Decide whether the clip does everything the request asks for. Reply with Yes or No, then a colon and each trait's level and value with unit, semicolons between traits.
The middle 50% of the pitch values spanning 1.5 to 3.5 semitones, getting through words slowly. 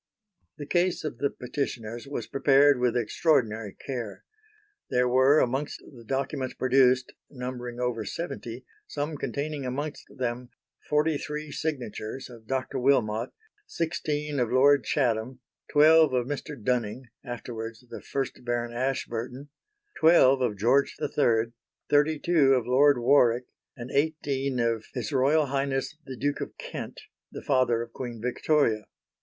Yes: average, 3.1 semitones; slow, 130 wpm